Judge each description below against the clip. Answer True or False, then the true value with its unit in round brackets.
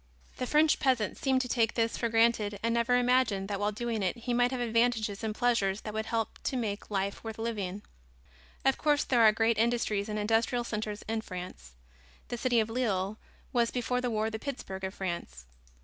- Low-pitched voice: False (225 Hz)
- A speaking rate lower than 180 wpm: False (200 wpm)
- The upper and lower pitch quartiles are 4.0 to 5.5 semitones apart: False (2.8 semitones)